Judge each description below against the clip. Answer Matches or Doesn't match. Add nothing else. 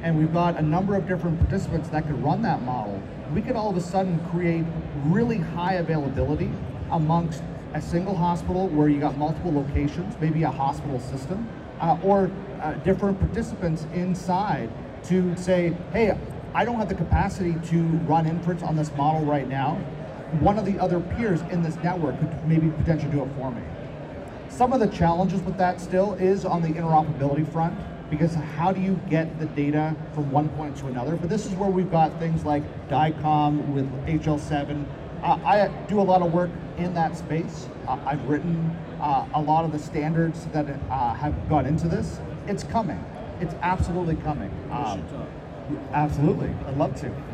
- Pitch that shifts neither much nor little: Matches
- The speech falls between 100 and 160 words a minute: Doesn't match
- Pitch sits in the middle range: Matches